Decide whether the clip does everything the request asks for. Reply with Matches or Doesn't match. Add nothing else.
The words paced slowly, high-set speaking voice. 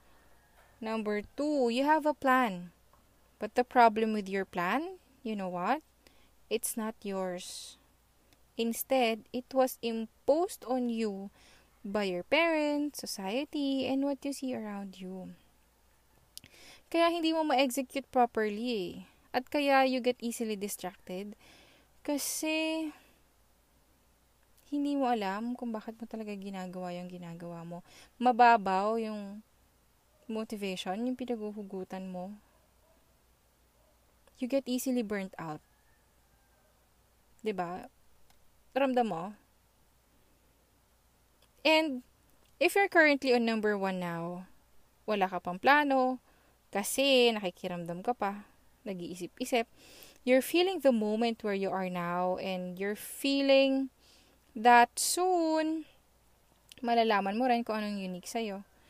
Matches